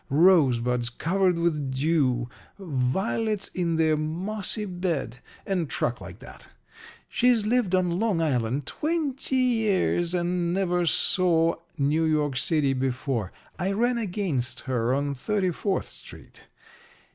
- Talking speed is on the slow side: Yes, slow, 125 wpm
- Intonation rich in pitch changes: Yes, wide, 5.9 semitones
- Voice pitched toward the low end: No, medium, 170 Hz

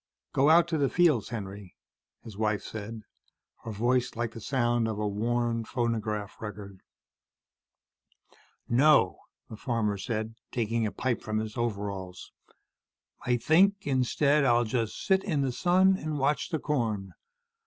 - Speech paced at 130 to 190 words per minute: Yes, average, 145 wpm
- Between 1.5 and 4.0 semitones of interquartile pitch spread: No, average, 4.4 semitones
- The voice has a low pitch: Yes, low, 120 Hz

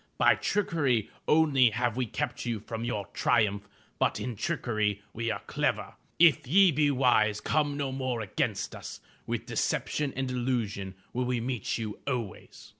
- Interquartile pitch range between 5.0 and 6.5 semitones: No, average, 3.9 semitones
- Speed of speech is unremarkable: Yes, average, 160 wpm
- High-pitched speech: No, low, 125 Hz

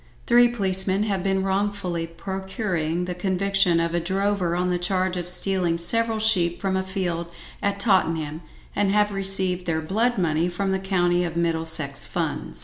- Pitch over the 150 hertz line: Yes, medium, 185 Hz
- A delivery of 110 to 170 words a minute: Yes, average, 165 wpm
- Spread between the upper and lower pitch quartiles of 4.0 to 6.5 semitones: No, narrow, 2.5 semitones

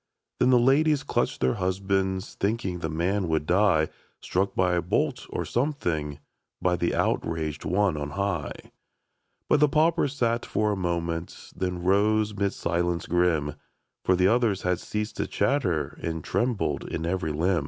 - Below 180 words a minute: Yes, average, 165 wpm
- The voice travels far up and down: No, average, 4.2 semitones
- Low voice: Yes, very low, 95 Hz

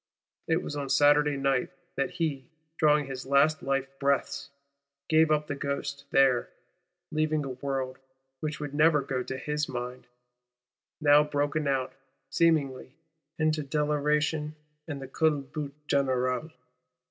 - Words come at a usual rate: No, slow, 125 wpm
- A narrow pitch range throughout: Yes, narrow, 1.8 semitones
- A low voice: No, medium, 145 Hz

